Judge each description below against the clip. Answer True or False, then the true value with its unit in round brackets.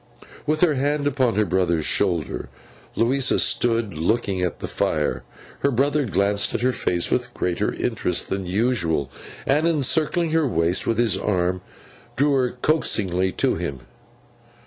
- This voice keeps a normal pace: True (150 wpm)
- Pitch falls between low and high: False (115 Hz)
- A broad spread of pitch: True (7.2 semitones)